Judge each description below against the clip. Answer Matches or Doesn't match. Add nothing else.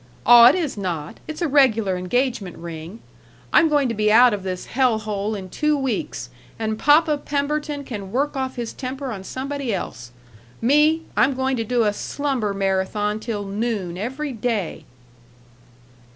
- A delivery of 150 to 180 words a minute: Matches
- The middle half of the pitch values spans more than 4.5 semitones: Matches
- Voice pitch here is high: Matches